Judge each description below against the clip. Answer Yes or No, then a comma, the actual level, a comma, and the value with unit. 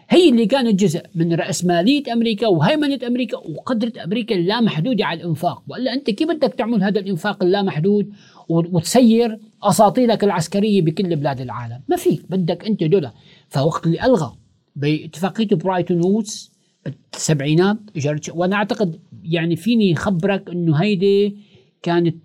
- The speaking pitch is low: No, high, 195 Hz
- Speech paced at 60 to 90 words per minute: No, average, 130 wpm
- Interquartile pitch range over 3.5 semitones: Yes, average, 4.8 semitones